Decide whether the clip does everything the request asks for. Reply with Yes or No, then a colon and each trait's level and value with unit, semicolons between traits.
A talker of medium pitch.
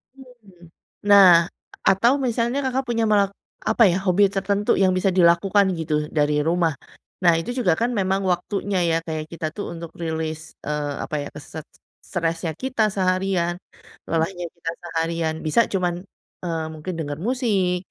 Yes: medium, 180 Hz